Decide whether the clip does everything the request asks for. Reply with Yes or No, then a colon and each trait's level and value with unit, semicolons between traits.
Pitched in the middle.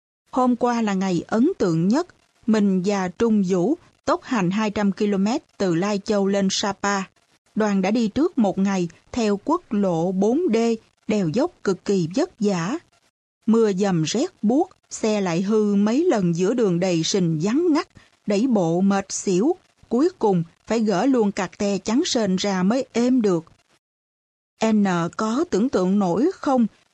No: high, 210 Hz